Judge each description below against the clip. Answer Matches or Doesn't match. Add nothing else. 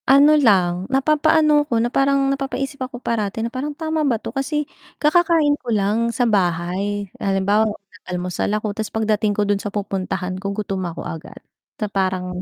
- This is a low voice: Doesn't match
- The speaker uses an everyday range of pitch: Doesn't match